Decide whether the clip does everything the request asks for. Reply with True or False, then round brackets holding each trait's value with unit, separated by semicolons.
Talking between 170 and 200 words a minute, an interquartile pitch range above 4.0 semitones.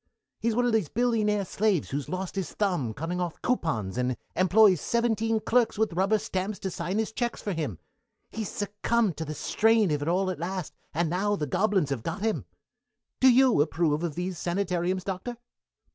True (190 wpm; 4.5 semitones)